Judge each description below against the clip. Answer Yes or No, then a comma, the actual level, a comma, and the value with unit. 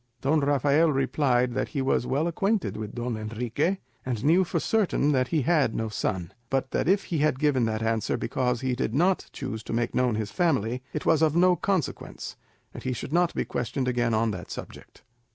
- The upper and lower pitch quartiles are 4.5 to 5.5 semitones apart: Yes, average, 5.1 semitones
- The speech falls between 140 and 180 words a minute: No, fast, 205 wpm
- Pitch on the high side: No, low, 130 Hz